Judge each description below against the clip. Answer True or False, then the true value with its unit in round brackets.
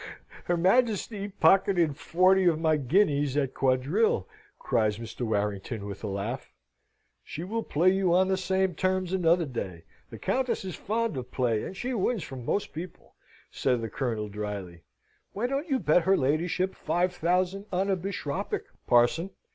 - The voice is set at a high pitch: False (170 Hz)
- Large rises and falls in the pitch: True (7.3 semitones)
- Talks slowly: False (165 wpm)